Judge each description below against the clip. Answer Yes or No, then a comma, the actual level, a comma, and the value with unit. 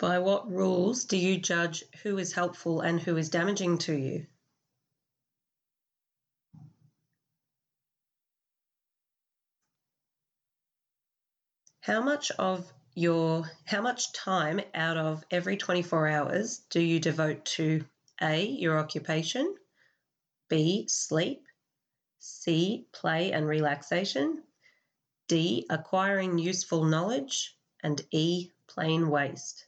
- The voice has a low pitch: No, medium, 165 Hz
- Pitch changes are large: No, average, 3.3 semitones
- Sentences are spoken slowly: Yes, slow, 95 wpm